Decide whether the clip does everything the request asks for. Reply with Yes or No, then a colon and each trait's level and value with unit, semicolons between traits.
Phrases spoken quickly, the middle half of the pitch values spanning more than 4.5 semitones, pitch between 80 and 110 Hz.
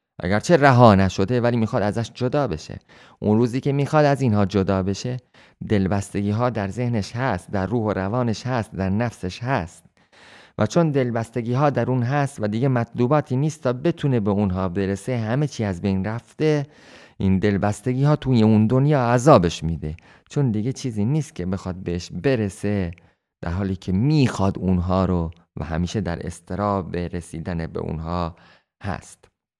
Yes: fast, 160 wpm; average, 5.1 semitones; low, 105 Hz